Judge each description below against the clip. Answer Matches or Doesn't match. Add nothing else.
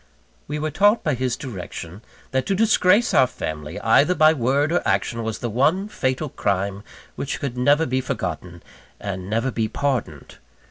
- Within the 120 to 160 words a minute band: Doesn't match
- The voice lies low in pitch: Matches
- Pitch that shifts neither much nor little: Doesn't match